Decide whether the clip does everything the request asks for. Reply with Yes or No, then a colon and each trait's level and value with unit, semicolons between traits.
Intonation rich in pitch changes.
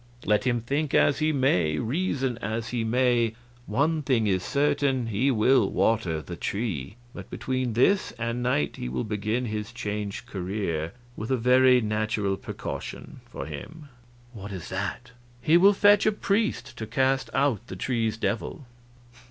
No: average, 4.2 semitones